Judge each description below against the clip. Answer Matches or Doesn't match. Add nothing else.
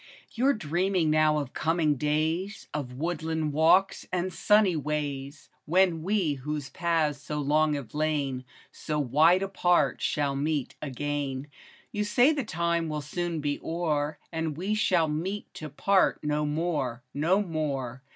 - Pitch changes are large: Doesn't match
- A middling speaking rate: Matches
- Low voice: Doesn't match